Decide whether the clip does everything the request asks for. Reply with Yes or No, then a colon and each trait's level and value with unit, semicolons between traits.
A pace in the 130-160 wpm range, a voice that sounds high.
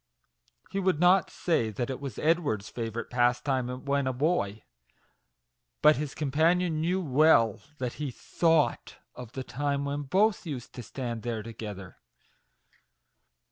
No: average, 140 wpm; medium, 140 Hz